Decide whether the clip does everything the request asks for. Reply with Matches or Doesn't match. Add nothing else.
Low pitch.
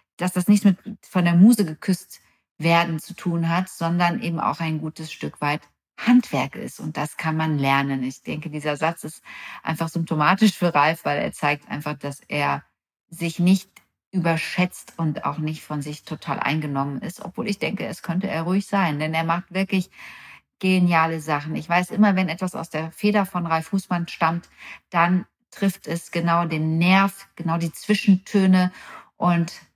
Doesn't match